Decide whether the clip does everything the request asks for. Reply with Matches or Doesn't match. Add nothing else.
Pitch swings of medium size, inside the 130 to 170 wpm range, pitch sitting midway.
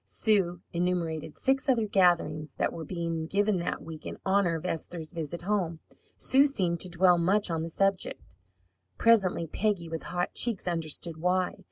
Matches